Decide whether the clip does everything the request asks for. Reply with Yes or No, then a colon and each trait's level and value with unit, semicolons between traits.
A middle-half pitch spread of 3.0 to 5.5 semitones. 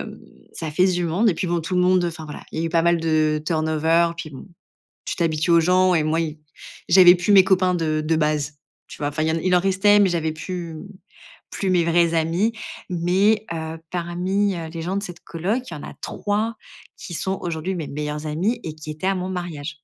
No: narrow, 2.6 semitones